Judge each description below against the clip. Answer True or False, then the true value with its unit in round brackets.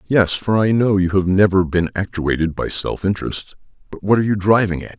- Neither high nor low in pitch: False (95 Hz)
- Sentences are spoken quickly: True (215 wpm)